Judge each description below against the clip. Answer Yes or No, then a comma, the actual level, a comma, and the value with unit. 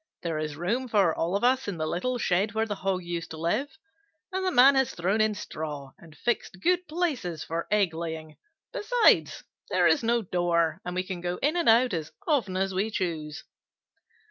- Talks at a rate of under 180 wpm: No, average, 200 wpm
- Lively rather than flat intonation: Yes, wide, 6.6 semitones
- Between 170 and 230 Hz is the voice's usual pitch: Yes, high, 190 Hz